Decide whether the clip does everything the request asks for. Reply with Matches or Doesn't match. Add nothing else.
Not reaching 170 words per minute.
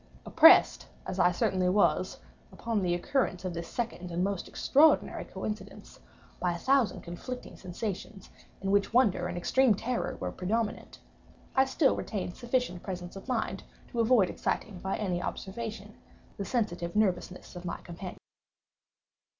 Matches